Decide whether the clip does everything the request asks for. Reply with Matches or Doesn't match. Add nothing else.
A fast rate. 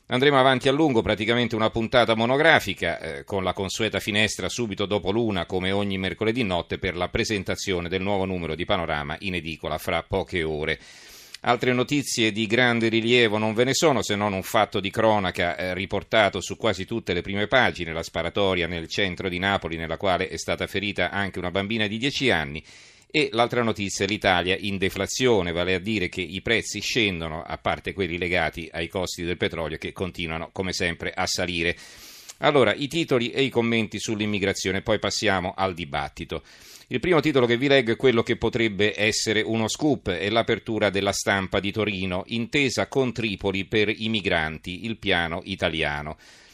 Matches